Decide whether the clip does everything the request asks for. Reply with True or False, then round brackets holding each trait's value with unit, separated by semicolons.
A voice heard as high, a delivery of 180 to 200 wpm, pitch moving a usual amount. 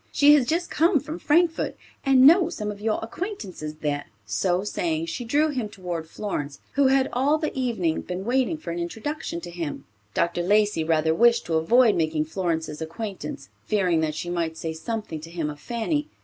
False (205 Hz; 190 wpm; 8.4 semitones)